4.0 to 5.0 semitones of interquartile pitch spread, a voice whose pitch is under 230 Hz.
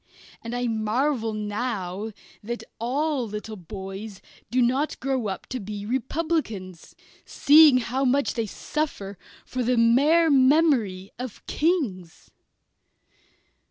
No: average, 4.7 semitones; high, 235 Hz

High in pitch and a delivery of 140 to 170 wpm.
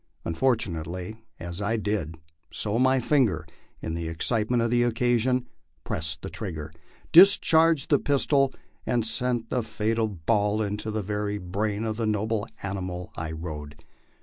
No: low, 110 Hz; average, 145 wpm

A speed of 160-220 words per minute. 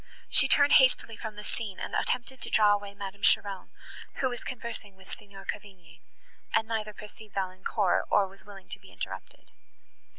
Yes: average, 170 wpm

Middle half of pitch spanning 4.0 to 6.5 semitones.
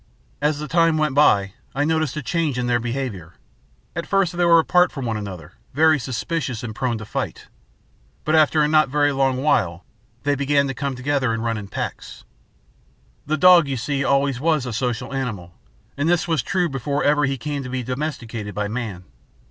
Yes: average, 4.3 semitones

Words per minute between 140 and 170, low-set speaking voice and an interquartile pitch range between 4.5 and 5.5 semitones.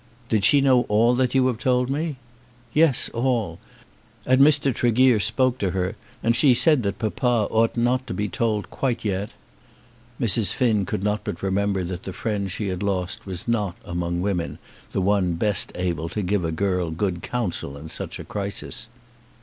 No: average, 180 wpm; low, 105 Hz; average, 4.8 semitones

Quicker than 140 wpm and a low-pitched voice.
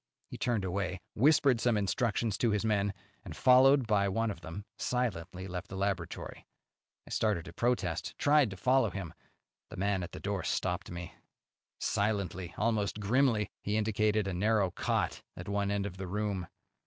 Yes: average, 170 wpm; low, 100 Hz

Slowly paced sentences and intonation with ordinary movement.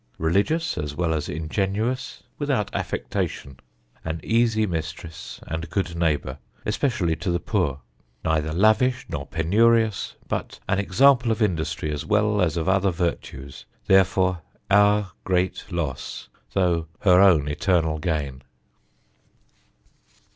Yes: slow, 120 wpm; average, 4.6 semitones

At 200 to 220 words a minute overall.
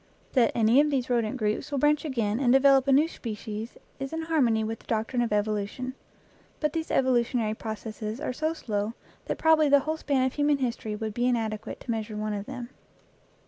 Yes: fast, 205 wpm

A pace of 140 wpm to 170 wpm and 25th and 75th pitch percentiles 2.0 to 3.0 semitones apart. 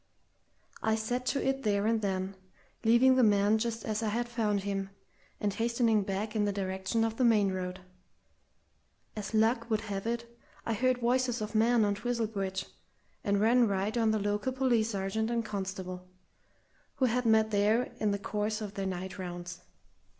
No: average, 180 wpm; average, 2.7 semitones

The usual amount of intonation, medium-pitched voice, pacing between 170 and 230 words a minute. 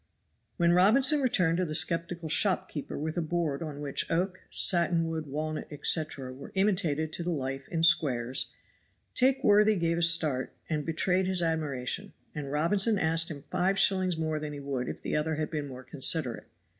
Yes: average, 3.4 semitones; medium, 165 Hz; average, 180 wpm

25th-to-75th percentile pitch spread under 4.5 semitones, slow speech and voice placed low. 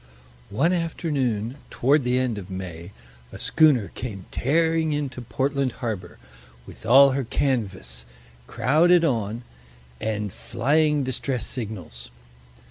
No: wide, 5.6 semitones; slow, 115 wpm; low, 125 Hz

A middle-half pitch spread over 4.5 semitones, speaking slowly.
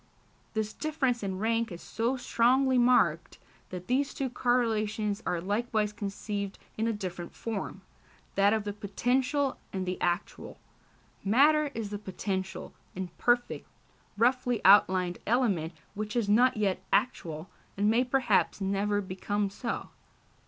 No: average, 3.8 semitones; slow, 130 wpm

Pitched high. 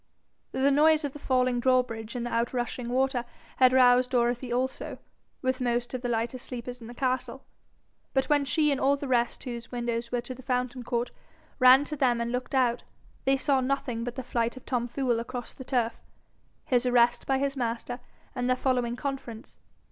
Yes: very high, 250 Hz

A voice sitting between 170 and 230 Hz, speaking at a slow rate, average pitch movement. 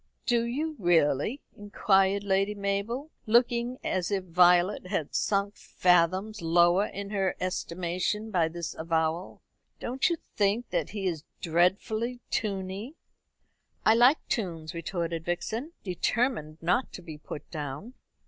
Yes: high, 190 Hz; slow, 130 wpm; average, 4.2 semitones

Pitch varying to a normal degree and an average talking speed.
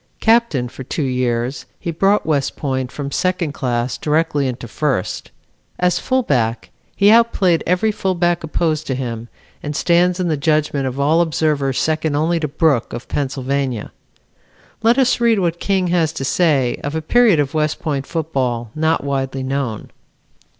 Yes: average, 4.5 semitones; average, 160 wpm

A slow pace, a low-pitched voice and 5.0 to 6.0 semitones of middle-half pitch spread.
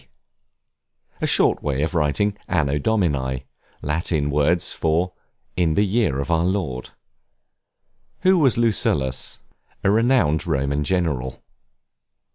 Yes: slow, 115 wpm; very low, 80 Hz; wide, 5.5 semitones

